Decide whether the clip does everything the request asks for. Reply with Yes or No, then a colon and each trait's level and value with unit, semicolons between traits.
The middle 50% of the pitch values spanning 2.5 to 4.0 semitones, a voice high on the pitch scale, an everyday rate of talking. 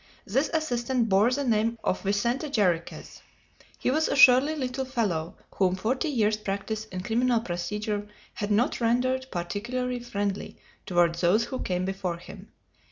No: average, 4.5 semitones; high, 220 Hz; average, 150 wpm